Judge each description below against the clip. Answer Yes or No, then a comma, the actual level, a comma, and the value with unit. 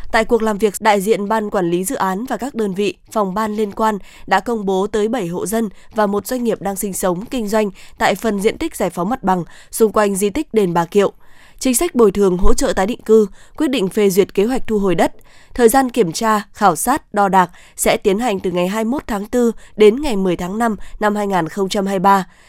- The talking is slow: No, average, 245 wpm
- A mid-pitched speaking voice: No, high, 210 Hz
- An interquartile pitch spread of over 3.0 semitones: No, narrow, 2.4 semitones